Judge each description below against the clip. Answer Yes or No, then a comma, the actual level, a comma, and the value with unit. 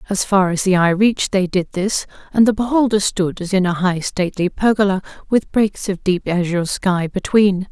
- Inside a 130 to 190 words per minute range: No, average, 200 wpm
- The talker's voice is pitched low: No, high, 190 Hz